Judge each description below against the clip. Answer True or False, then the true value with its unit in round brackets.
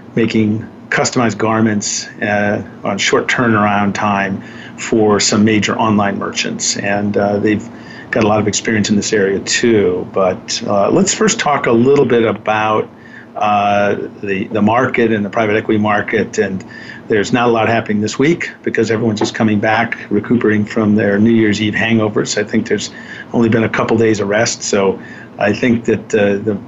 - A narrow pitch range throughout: True (1.8 semitones)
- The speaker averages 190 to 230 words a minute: False (180 wpm)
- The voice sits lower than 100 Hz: False (110 Hz)